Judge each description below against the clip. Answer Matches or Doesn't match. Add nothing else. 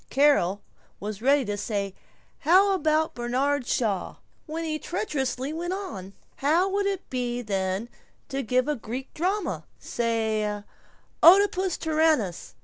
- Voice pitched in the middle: Doesn't match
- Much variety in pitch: Matches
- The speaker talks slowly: Matches